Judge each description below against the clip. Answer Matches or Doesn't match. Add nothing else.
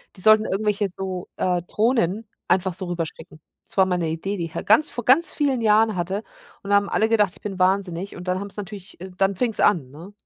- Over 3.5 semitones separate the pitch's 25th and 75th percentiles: Doesn't match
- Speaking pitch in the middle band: Doesn't match